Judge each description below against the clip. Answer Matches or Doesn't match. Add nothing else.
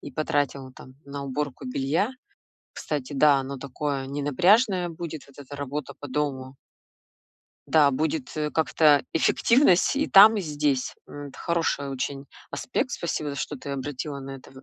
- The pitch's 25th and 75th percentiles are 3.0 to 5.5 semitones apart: Doesn't match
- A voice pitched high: Doesn't match